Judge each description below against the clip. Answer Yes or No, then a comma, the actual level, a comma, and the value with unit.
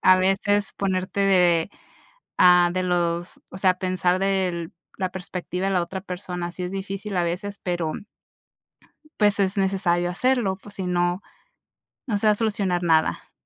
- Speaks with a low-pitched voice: No, medium, 185 Hz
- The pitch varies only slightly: Yes, narrow, 1.8 semitones